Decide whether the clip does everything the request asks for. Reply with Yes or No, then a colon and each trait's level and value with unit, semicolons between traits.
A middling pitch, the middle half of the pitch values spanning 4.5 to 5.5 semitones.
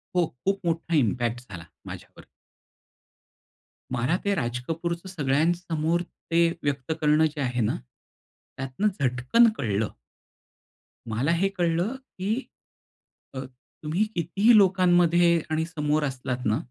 Yes: medium, 160 Hz; average, 5.2 semitones